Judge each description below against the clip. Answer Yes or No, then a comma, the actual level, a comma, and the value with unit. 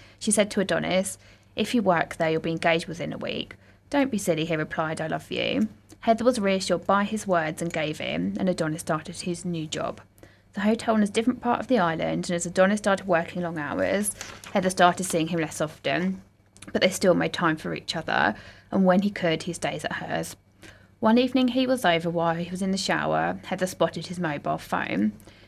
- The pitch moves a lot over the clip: No, average, 3.7 semitones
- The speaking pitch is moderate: Yes, medium, 180 Hz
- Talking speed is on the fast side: Yes, fast, 215 wpm